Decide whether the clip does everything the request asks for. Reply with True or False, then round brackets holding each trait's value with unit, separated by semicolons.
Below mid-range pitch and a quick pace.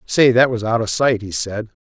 True (115 Hz; 260 wpm)